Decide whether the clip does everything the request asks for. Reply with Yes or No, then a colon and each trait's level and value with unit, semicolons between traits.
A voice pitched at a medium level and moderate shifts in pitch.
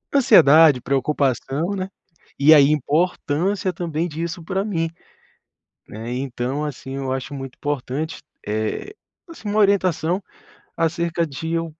Yes: medium, 155 Hz; average, 4.4 semitones